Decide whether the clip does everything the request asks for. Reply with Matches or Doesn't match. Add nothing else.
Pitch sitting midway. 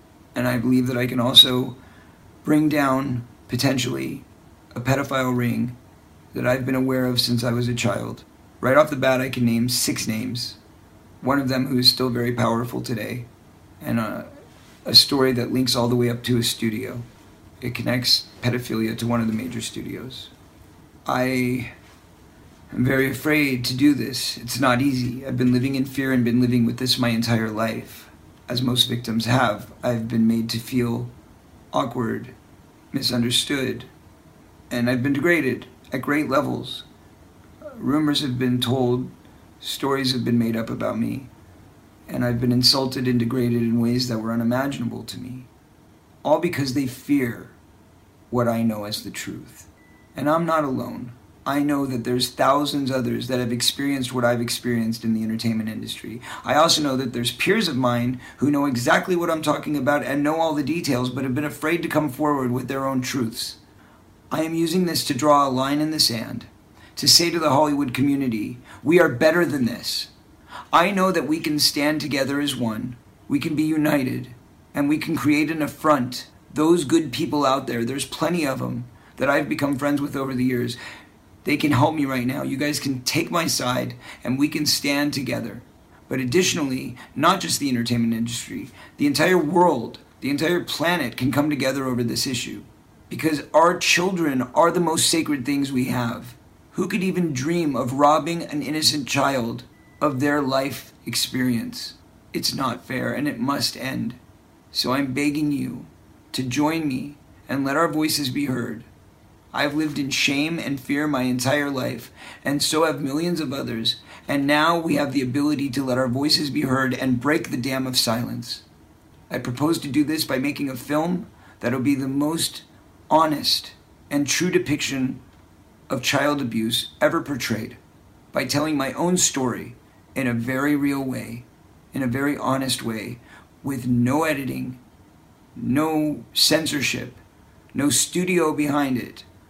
Doesn't match